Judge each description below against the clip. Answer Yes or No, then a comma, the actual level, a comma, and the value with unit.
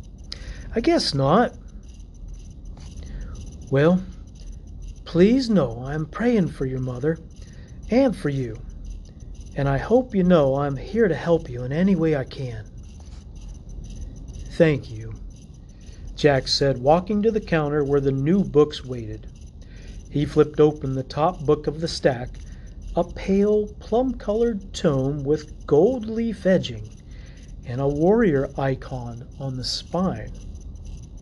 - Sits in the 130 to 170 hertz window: Yes, medium, 140 Hz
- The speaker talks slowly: Yes, slow, 130 wpm